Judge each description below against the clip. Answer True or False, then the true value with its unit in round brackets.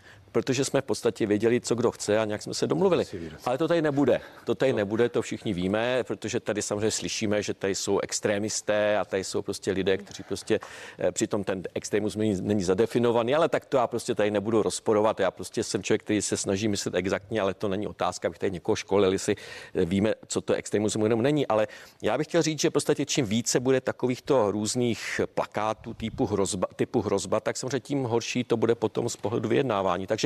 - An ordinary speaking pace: False (205 wpm)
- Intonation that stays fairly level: False (3.0 semitones)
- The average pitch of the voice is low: True (110 Hz)